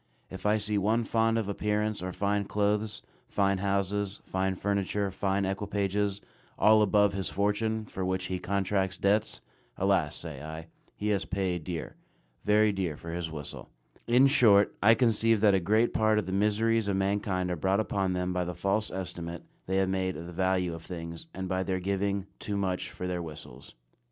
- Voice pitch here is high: No, low, 100 Hz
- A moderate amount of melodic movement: No, narrow, 2.1 semitones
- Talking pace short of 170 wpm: No, average, 185 wpm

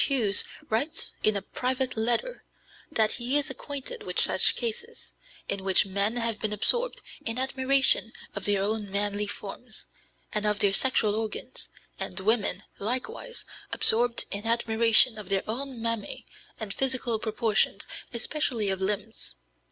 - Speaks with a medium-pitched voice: No, high, 225 Hz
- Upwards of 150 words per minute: No, average, 145 wpm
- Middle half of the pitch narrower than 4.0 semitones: Yes, average, 3.6 semitones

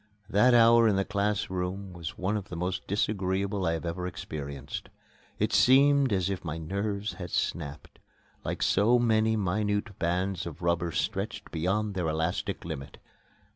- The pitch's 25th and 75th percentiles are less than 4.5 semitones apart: Yes, average, 3.6 semitones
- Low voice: Yes, very low, 95 Hz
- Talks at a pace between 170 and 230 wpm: No, average, 155 wpm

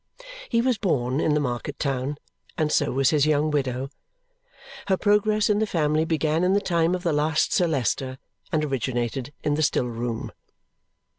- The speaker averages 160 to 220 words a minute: Yes, average, 175 wpm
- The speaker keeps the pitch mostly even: No, average, 4.5 semitones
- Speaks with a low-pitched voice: No, medium, 150 Hz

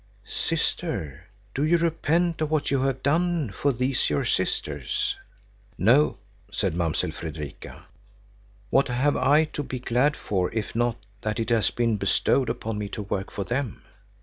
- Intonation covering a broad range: Yes, wide, 5.7 semitones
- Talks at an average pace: Yes, average, 155 wpm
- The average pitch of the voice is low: Yes, low, 125 Hz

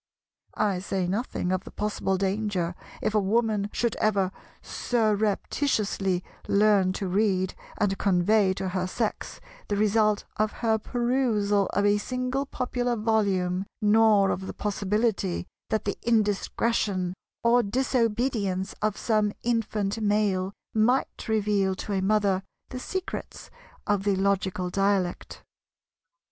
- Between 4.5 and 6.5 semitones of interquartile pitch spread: No, narrow, 2.4 semitones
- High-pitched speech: Yes, high, 205 Hz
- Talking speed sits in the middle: No, slow, 125 wpm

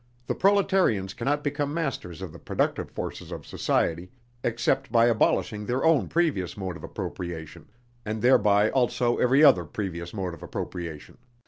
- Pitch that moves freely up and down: Yes, wide, 7.0 semitones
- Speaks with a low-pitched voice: Yes, low, 110 Hz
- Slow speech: No, average, 150 wpm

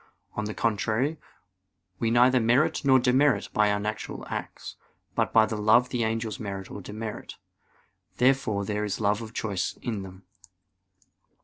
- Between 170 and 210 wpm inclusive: No, average, 150 wpm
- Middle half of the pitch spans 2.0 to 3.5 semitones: Yes, average, 2.9 semitones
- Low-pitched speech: Yes, low, 110 Hz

